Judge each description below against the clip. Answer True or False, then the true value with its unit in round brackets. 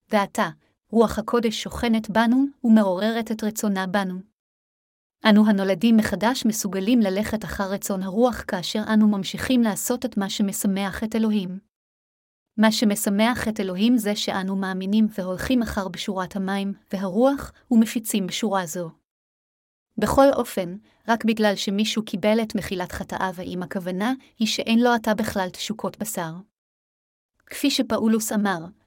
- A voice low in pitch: False (210 Hz)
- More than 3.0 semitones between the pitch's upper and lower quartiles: False (2.7 semitones)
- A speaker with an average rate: True (130 wpm)